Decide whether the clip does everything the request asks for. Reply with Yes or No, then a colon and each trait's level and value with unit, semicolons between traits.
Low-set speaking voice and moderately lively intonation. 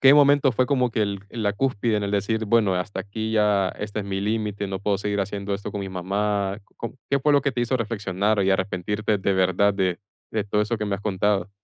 No: low, 105 Hz; narrow, 2.1 semitones